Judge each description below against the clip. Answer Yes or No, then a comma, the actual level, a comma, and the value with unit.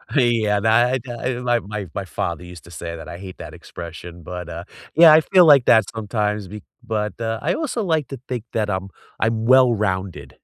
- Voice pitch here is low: Yes, low, 105 Hz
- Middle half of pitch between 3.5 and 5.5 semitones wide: Yes, average, 4.8 semitones